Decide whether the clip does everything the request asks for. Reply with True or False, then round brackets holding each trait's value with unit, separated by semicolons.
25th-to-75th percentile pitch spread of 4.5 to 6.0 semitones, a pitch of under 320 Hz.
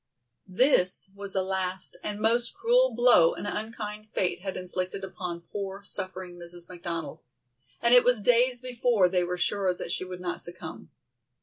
False (4.1 semitones; 190 Hz)